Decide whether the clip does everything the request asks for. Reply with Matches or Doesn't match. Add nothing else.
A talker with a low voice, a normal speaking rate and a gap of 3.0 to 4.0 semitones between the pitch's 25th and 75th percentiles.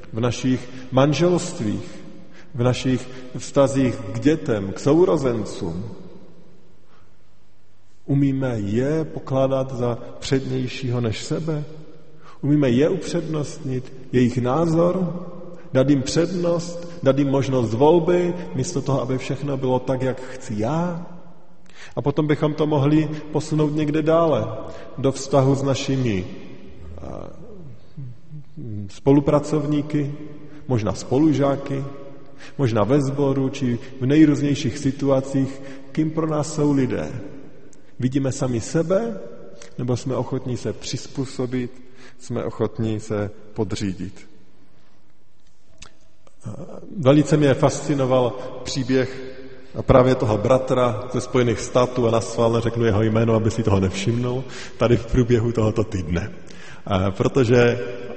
Doesn't match